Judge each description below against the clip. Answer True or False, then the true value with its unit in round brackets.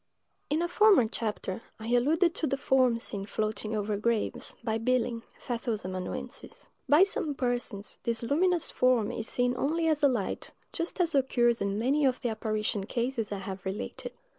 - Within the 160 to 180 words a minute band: True (170 wpm)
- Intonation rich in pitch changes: False (4.6 semitones)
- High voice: True (240 Hz)